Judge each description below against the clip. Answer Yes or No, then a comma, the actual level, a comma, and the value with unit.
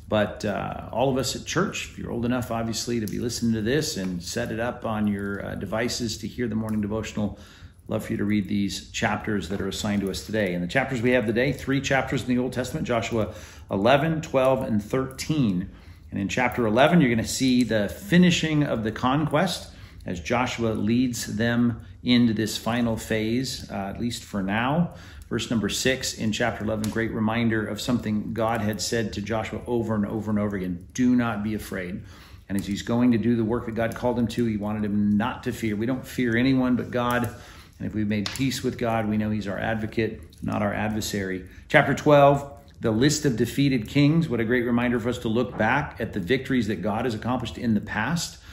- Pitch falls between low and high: No, low, 115 Hz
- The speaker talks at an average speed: No, fast, 220 wpm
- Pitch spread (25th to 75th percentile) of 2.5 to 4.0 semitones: Yes, average, 3.1 semitones